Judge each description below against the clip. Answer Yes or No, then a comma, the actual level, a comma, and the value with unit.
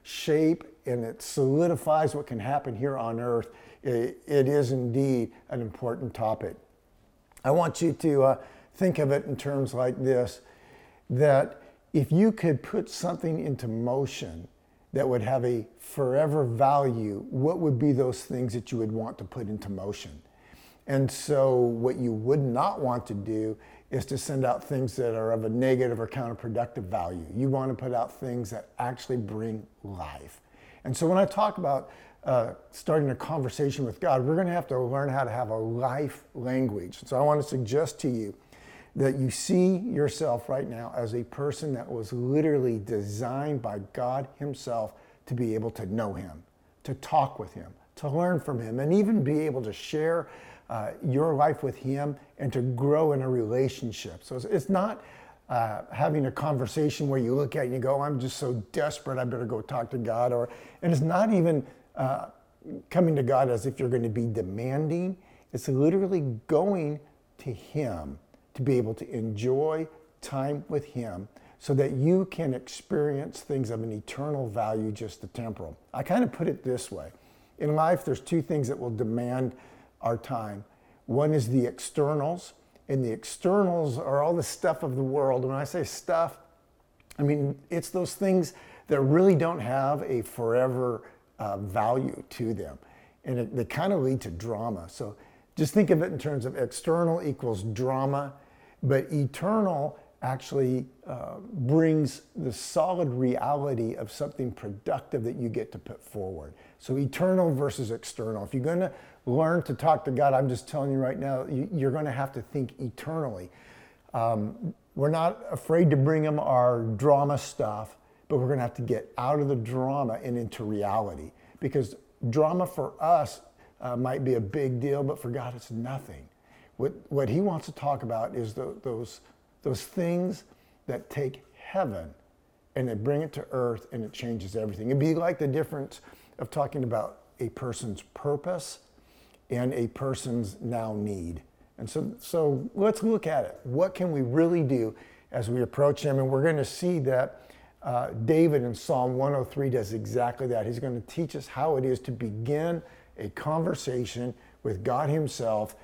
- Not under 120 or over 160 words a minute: No, average, 180 wpm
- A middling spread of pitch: Yes, average, 3.9 semitones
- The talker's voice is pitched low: Yes, low, 130 Hz